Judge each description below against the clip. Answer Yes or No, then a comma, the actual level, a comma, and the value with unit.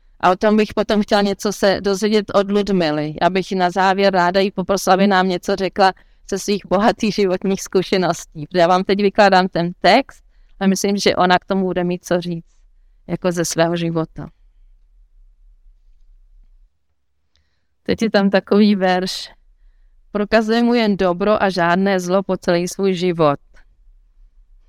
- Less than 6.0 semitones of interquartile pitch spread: No, wide, 8.7 semitones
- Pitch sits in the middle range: Yes, medium, 180 Hz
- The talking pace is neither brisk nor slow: Yes, average, 155 wpm